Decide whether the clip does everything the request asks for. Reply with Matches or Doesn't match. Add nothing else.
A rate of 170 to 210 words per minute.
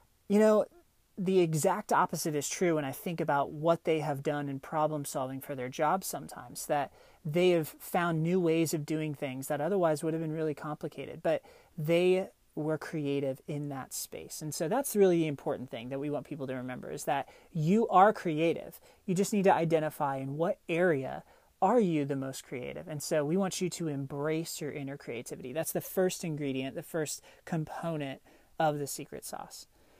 Matches